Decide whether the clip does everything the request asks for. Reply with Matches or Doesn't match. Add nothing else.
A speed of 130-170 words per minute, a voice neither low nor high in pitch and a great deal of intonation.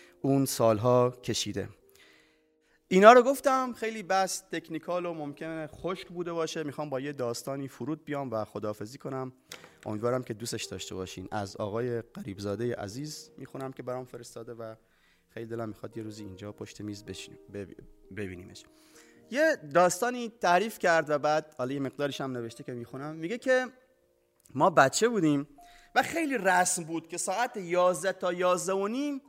Matches